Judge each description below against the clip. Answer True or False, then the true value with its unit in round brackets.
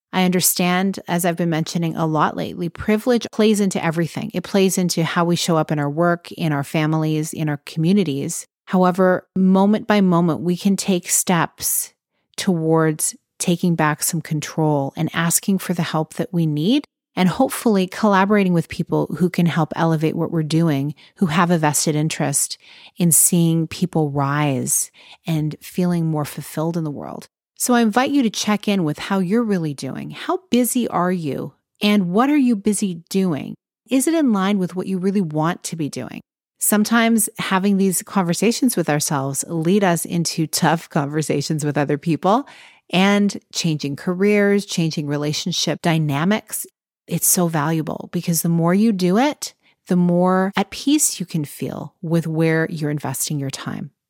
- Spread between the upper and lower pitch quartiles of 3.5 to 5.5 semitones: True (3.8 semitones)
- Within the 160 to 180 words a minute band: True (170 wpm)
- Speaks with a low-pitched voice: False (175 Hz)